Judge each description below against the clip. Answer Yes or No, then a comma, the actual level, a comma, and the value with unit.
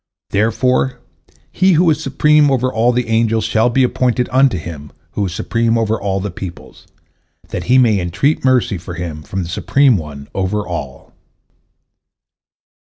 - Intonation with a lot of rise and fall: Yes, wide, 5.9 semitones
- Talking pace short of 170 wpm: Yes, average, 155 wpm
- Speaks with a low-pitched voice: Yes, low, 110 Hz